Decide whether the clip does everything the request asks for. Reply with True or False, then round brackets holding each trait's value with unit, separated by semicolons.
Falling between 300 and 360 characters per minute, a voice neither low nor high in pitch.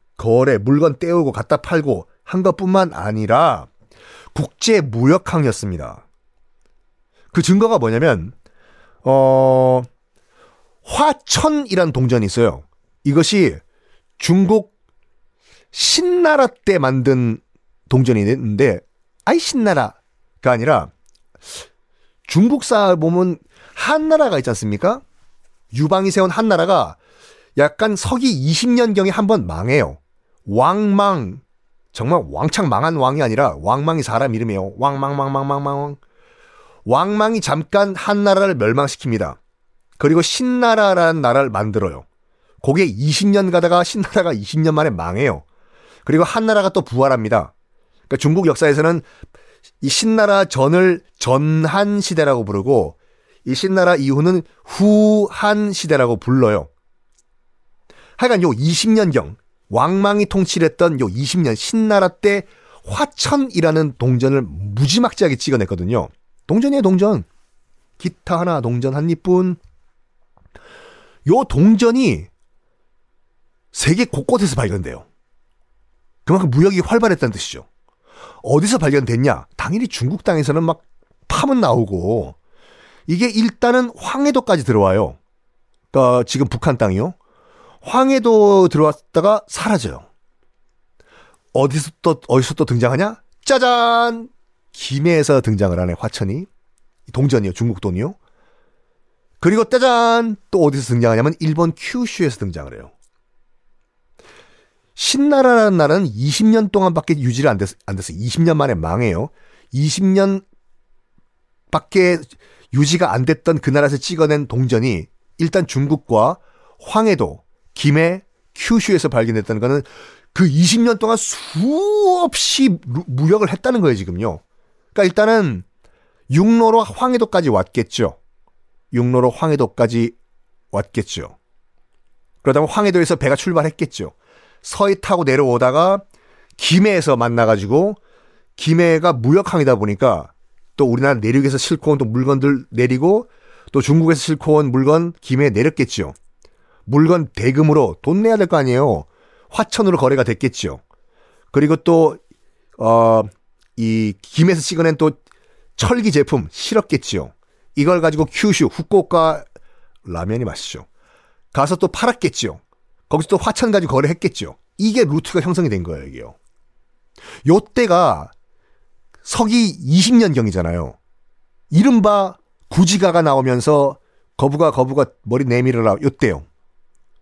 False (260 characters per minute; 155 Hz)